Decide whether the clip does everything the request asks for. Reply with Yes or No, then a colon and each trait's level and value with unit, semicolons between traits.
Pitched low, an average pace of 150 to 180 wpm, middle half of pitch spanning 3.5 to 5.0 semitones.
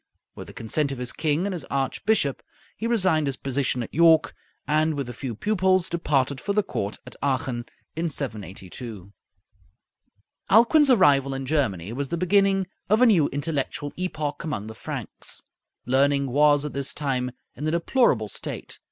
No: medium, 145 Hz; average, 165 wpm; average, 4.7 semitones